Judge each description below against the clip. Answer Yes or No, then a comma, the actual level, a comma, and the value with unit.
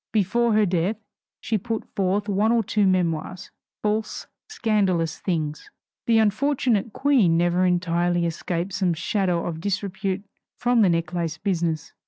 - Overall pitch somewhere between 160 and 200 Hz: Yes, high, 190 Hz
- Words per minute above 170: No, slow, 135 wpm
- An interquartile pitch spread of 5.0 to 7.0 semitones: No, average, 3.8 semitones